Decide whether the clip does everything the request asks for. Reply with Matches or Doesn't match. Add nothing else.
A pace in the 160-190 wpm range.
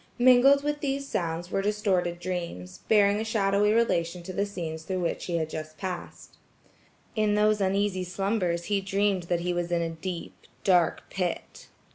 Matches